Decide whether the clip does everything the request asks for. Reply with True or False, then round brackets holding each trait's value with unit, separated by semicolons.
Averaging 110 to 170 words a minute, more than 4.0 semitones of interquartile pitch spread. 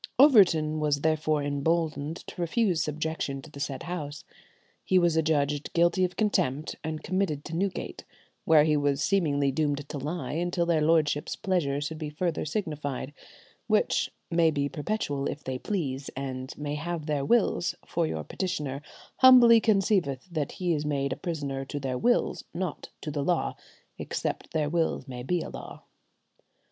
False (165 wpm; 3.3 semitones)